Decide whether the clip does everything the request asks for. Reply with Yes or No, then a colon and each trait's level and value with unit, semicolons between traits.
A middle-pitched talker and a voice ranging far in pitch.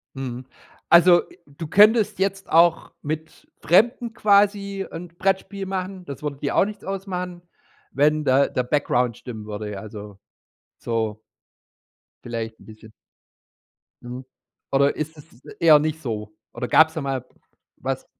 Yes: medium, 155 Hz; wide, 7.3 semitones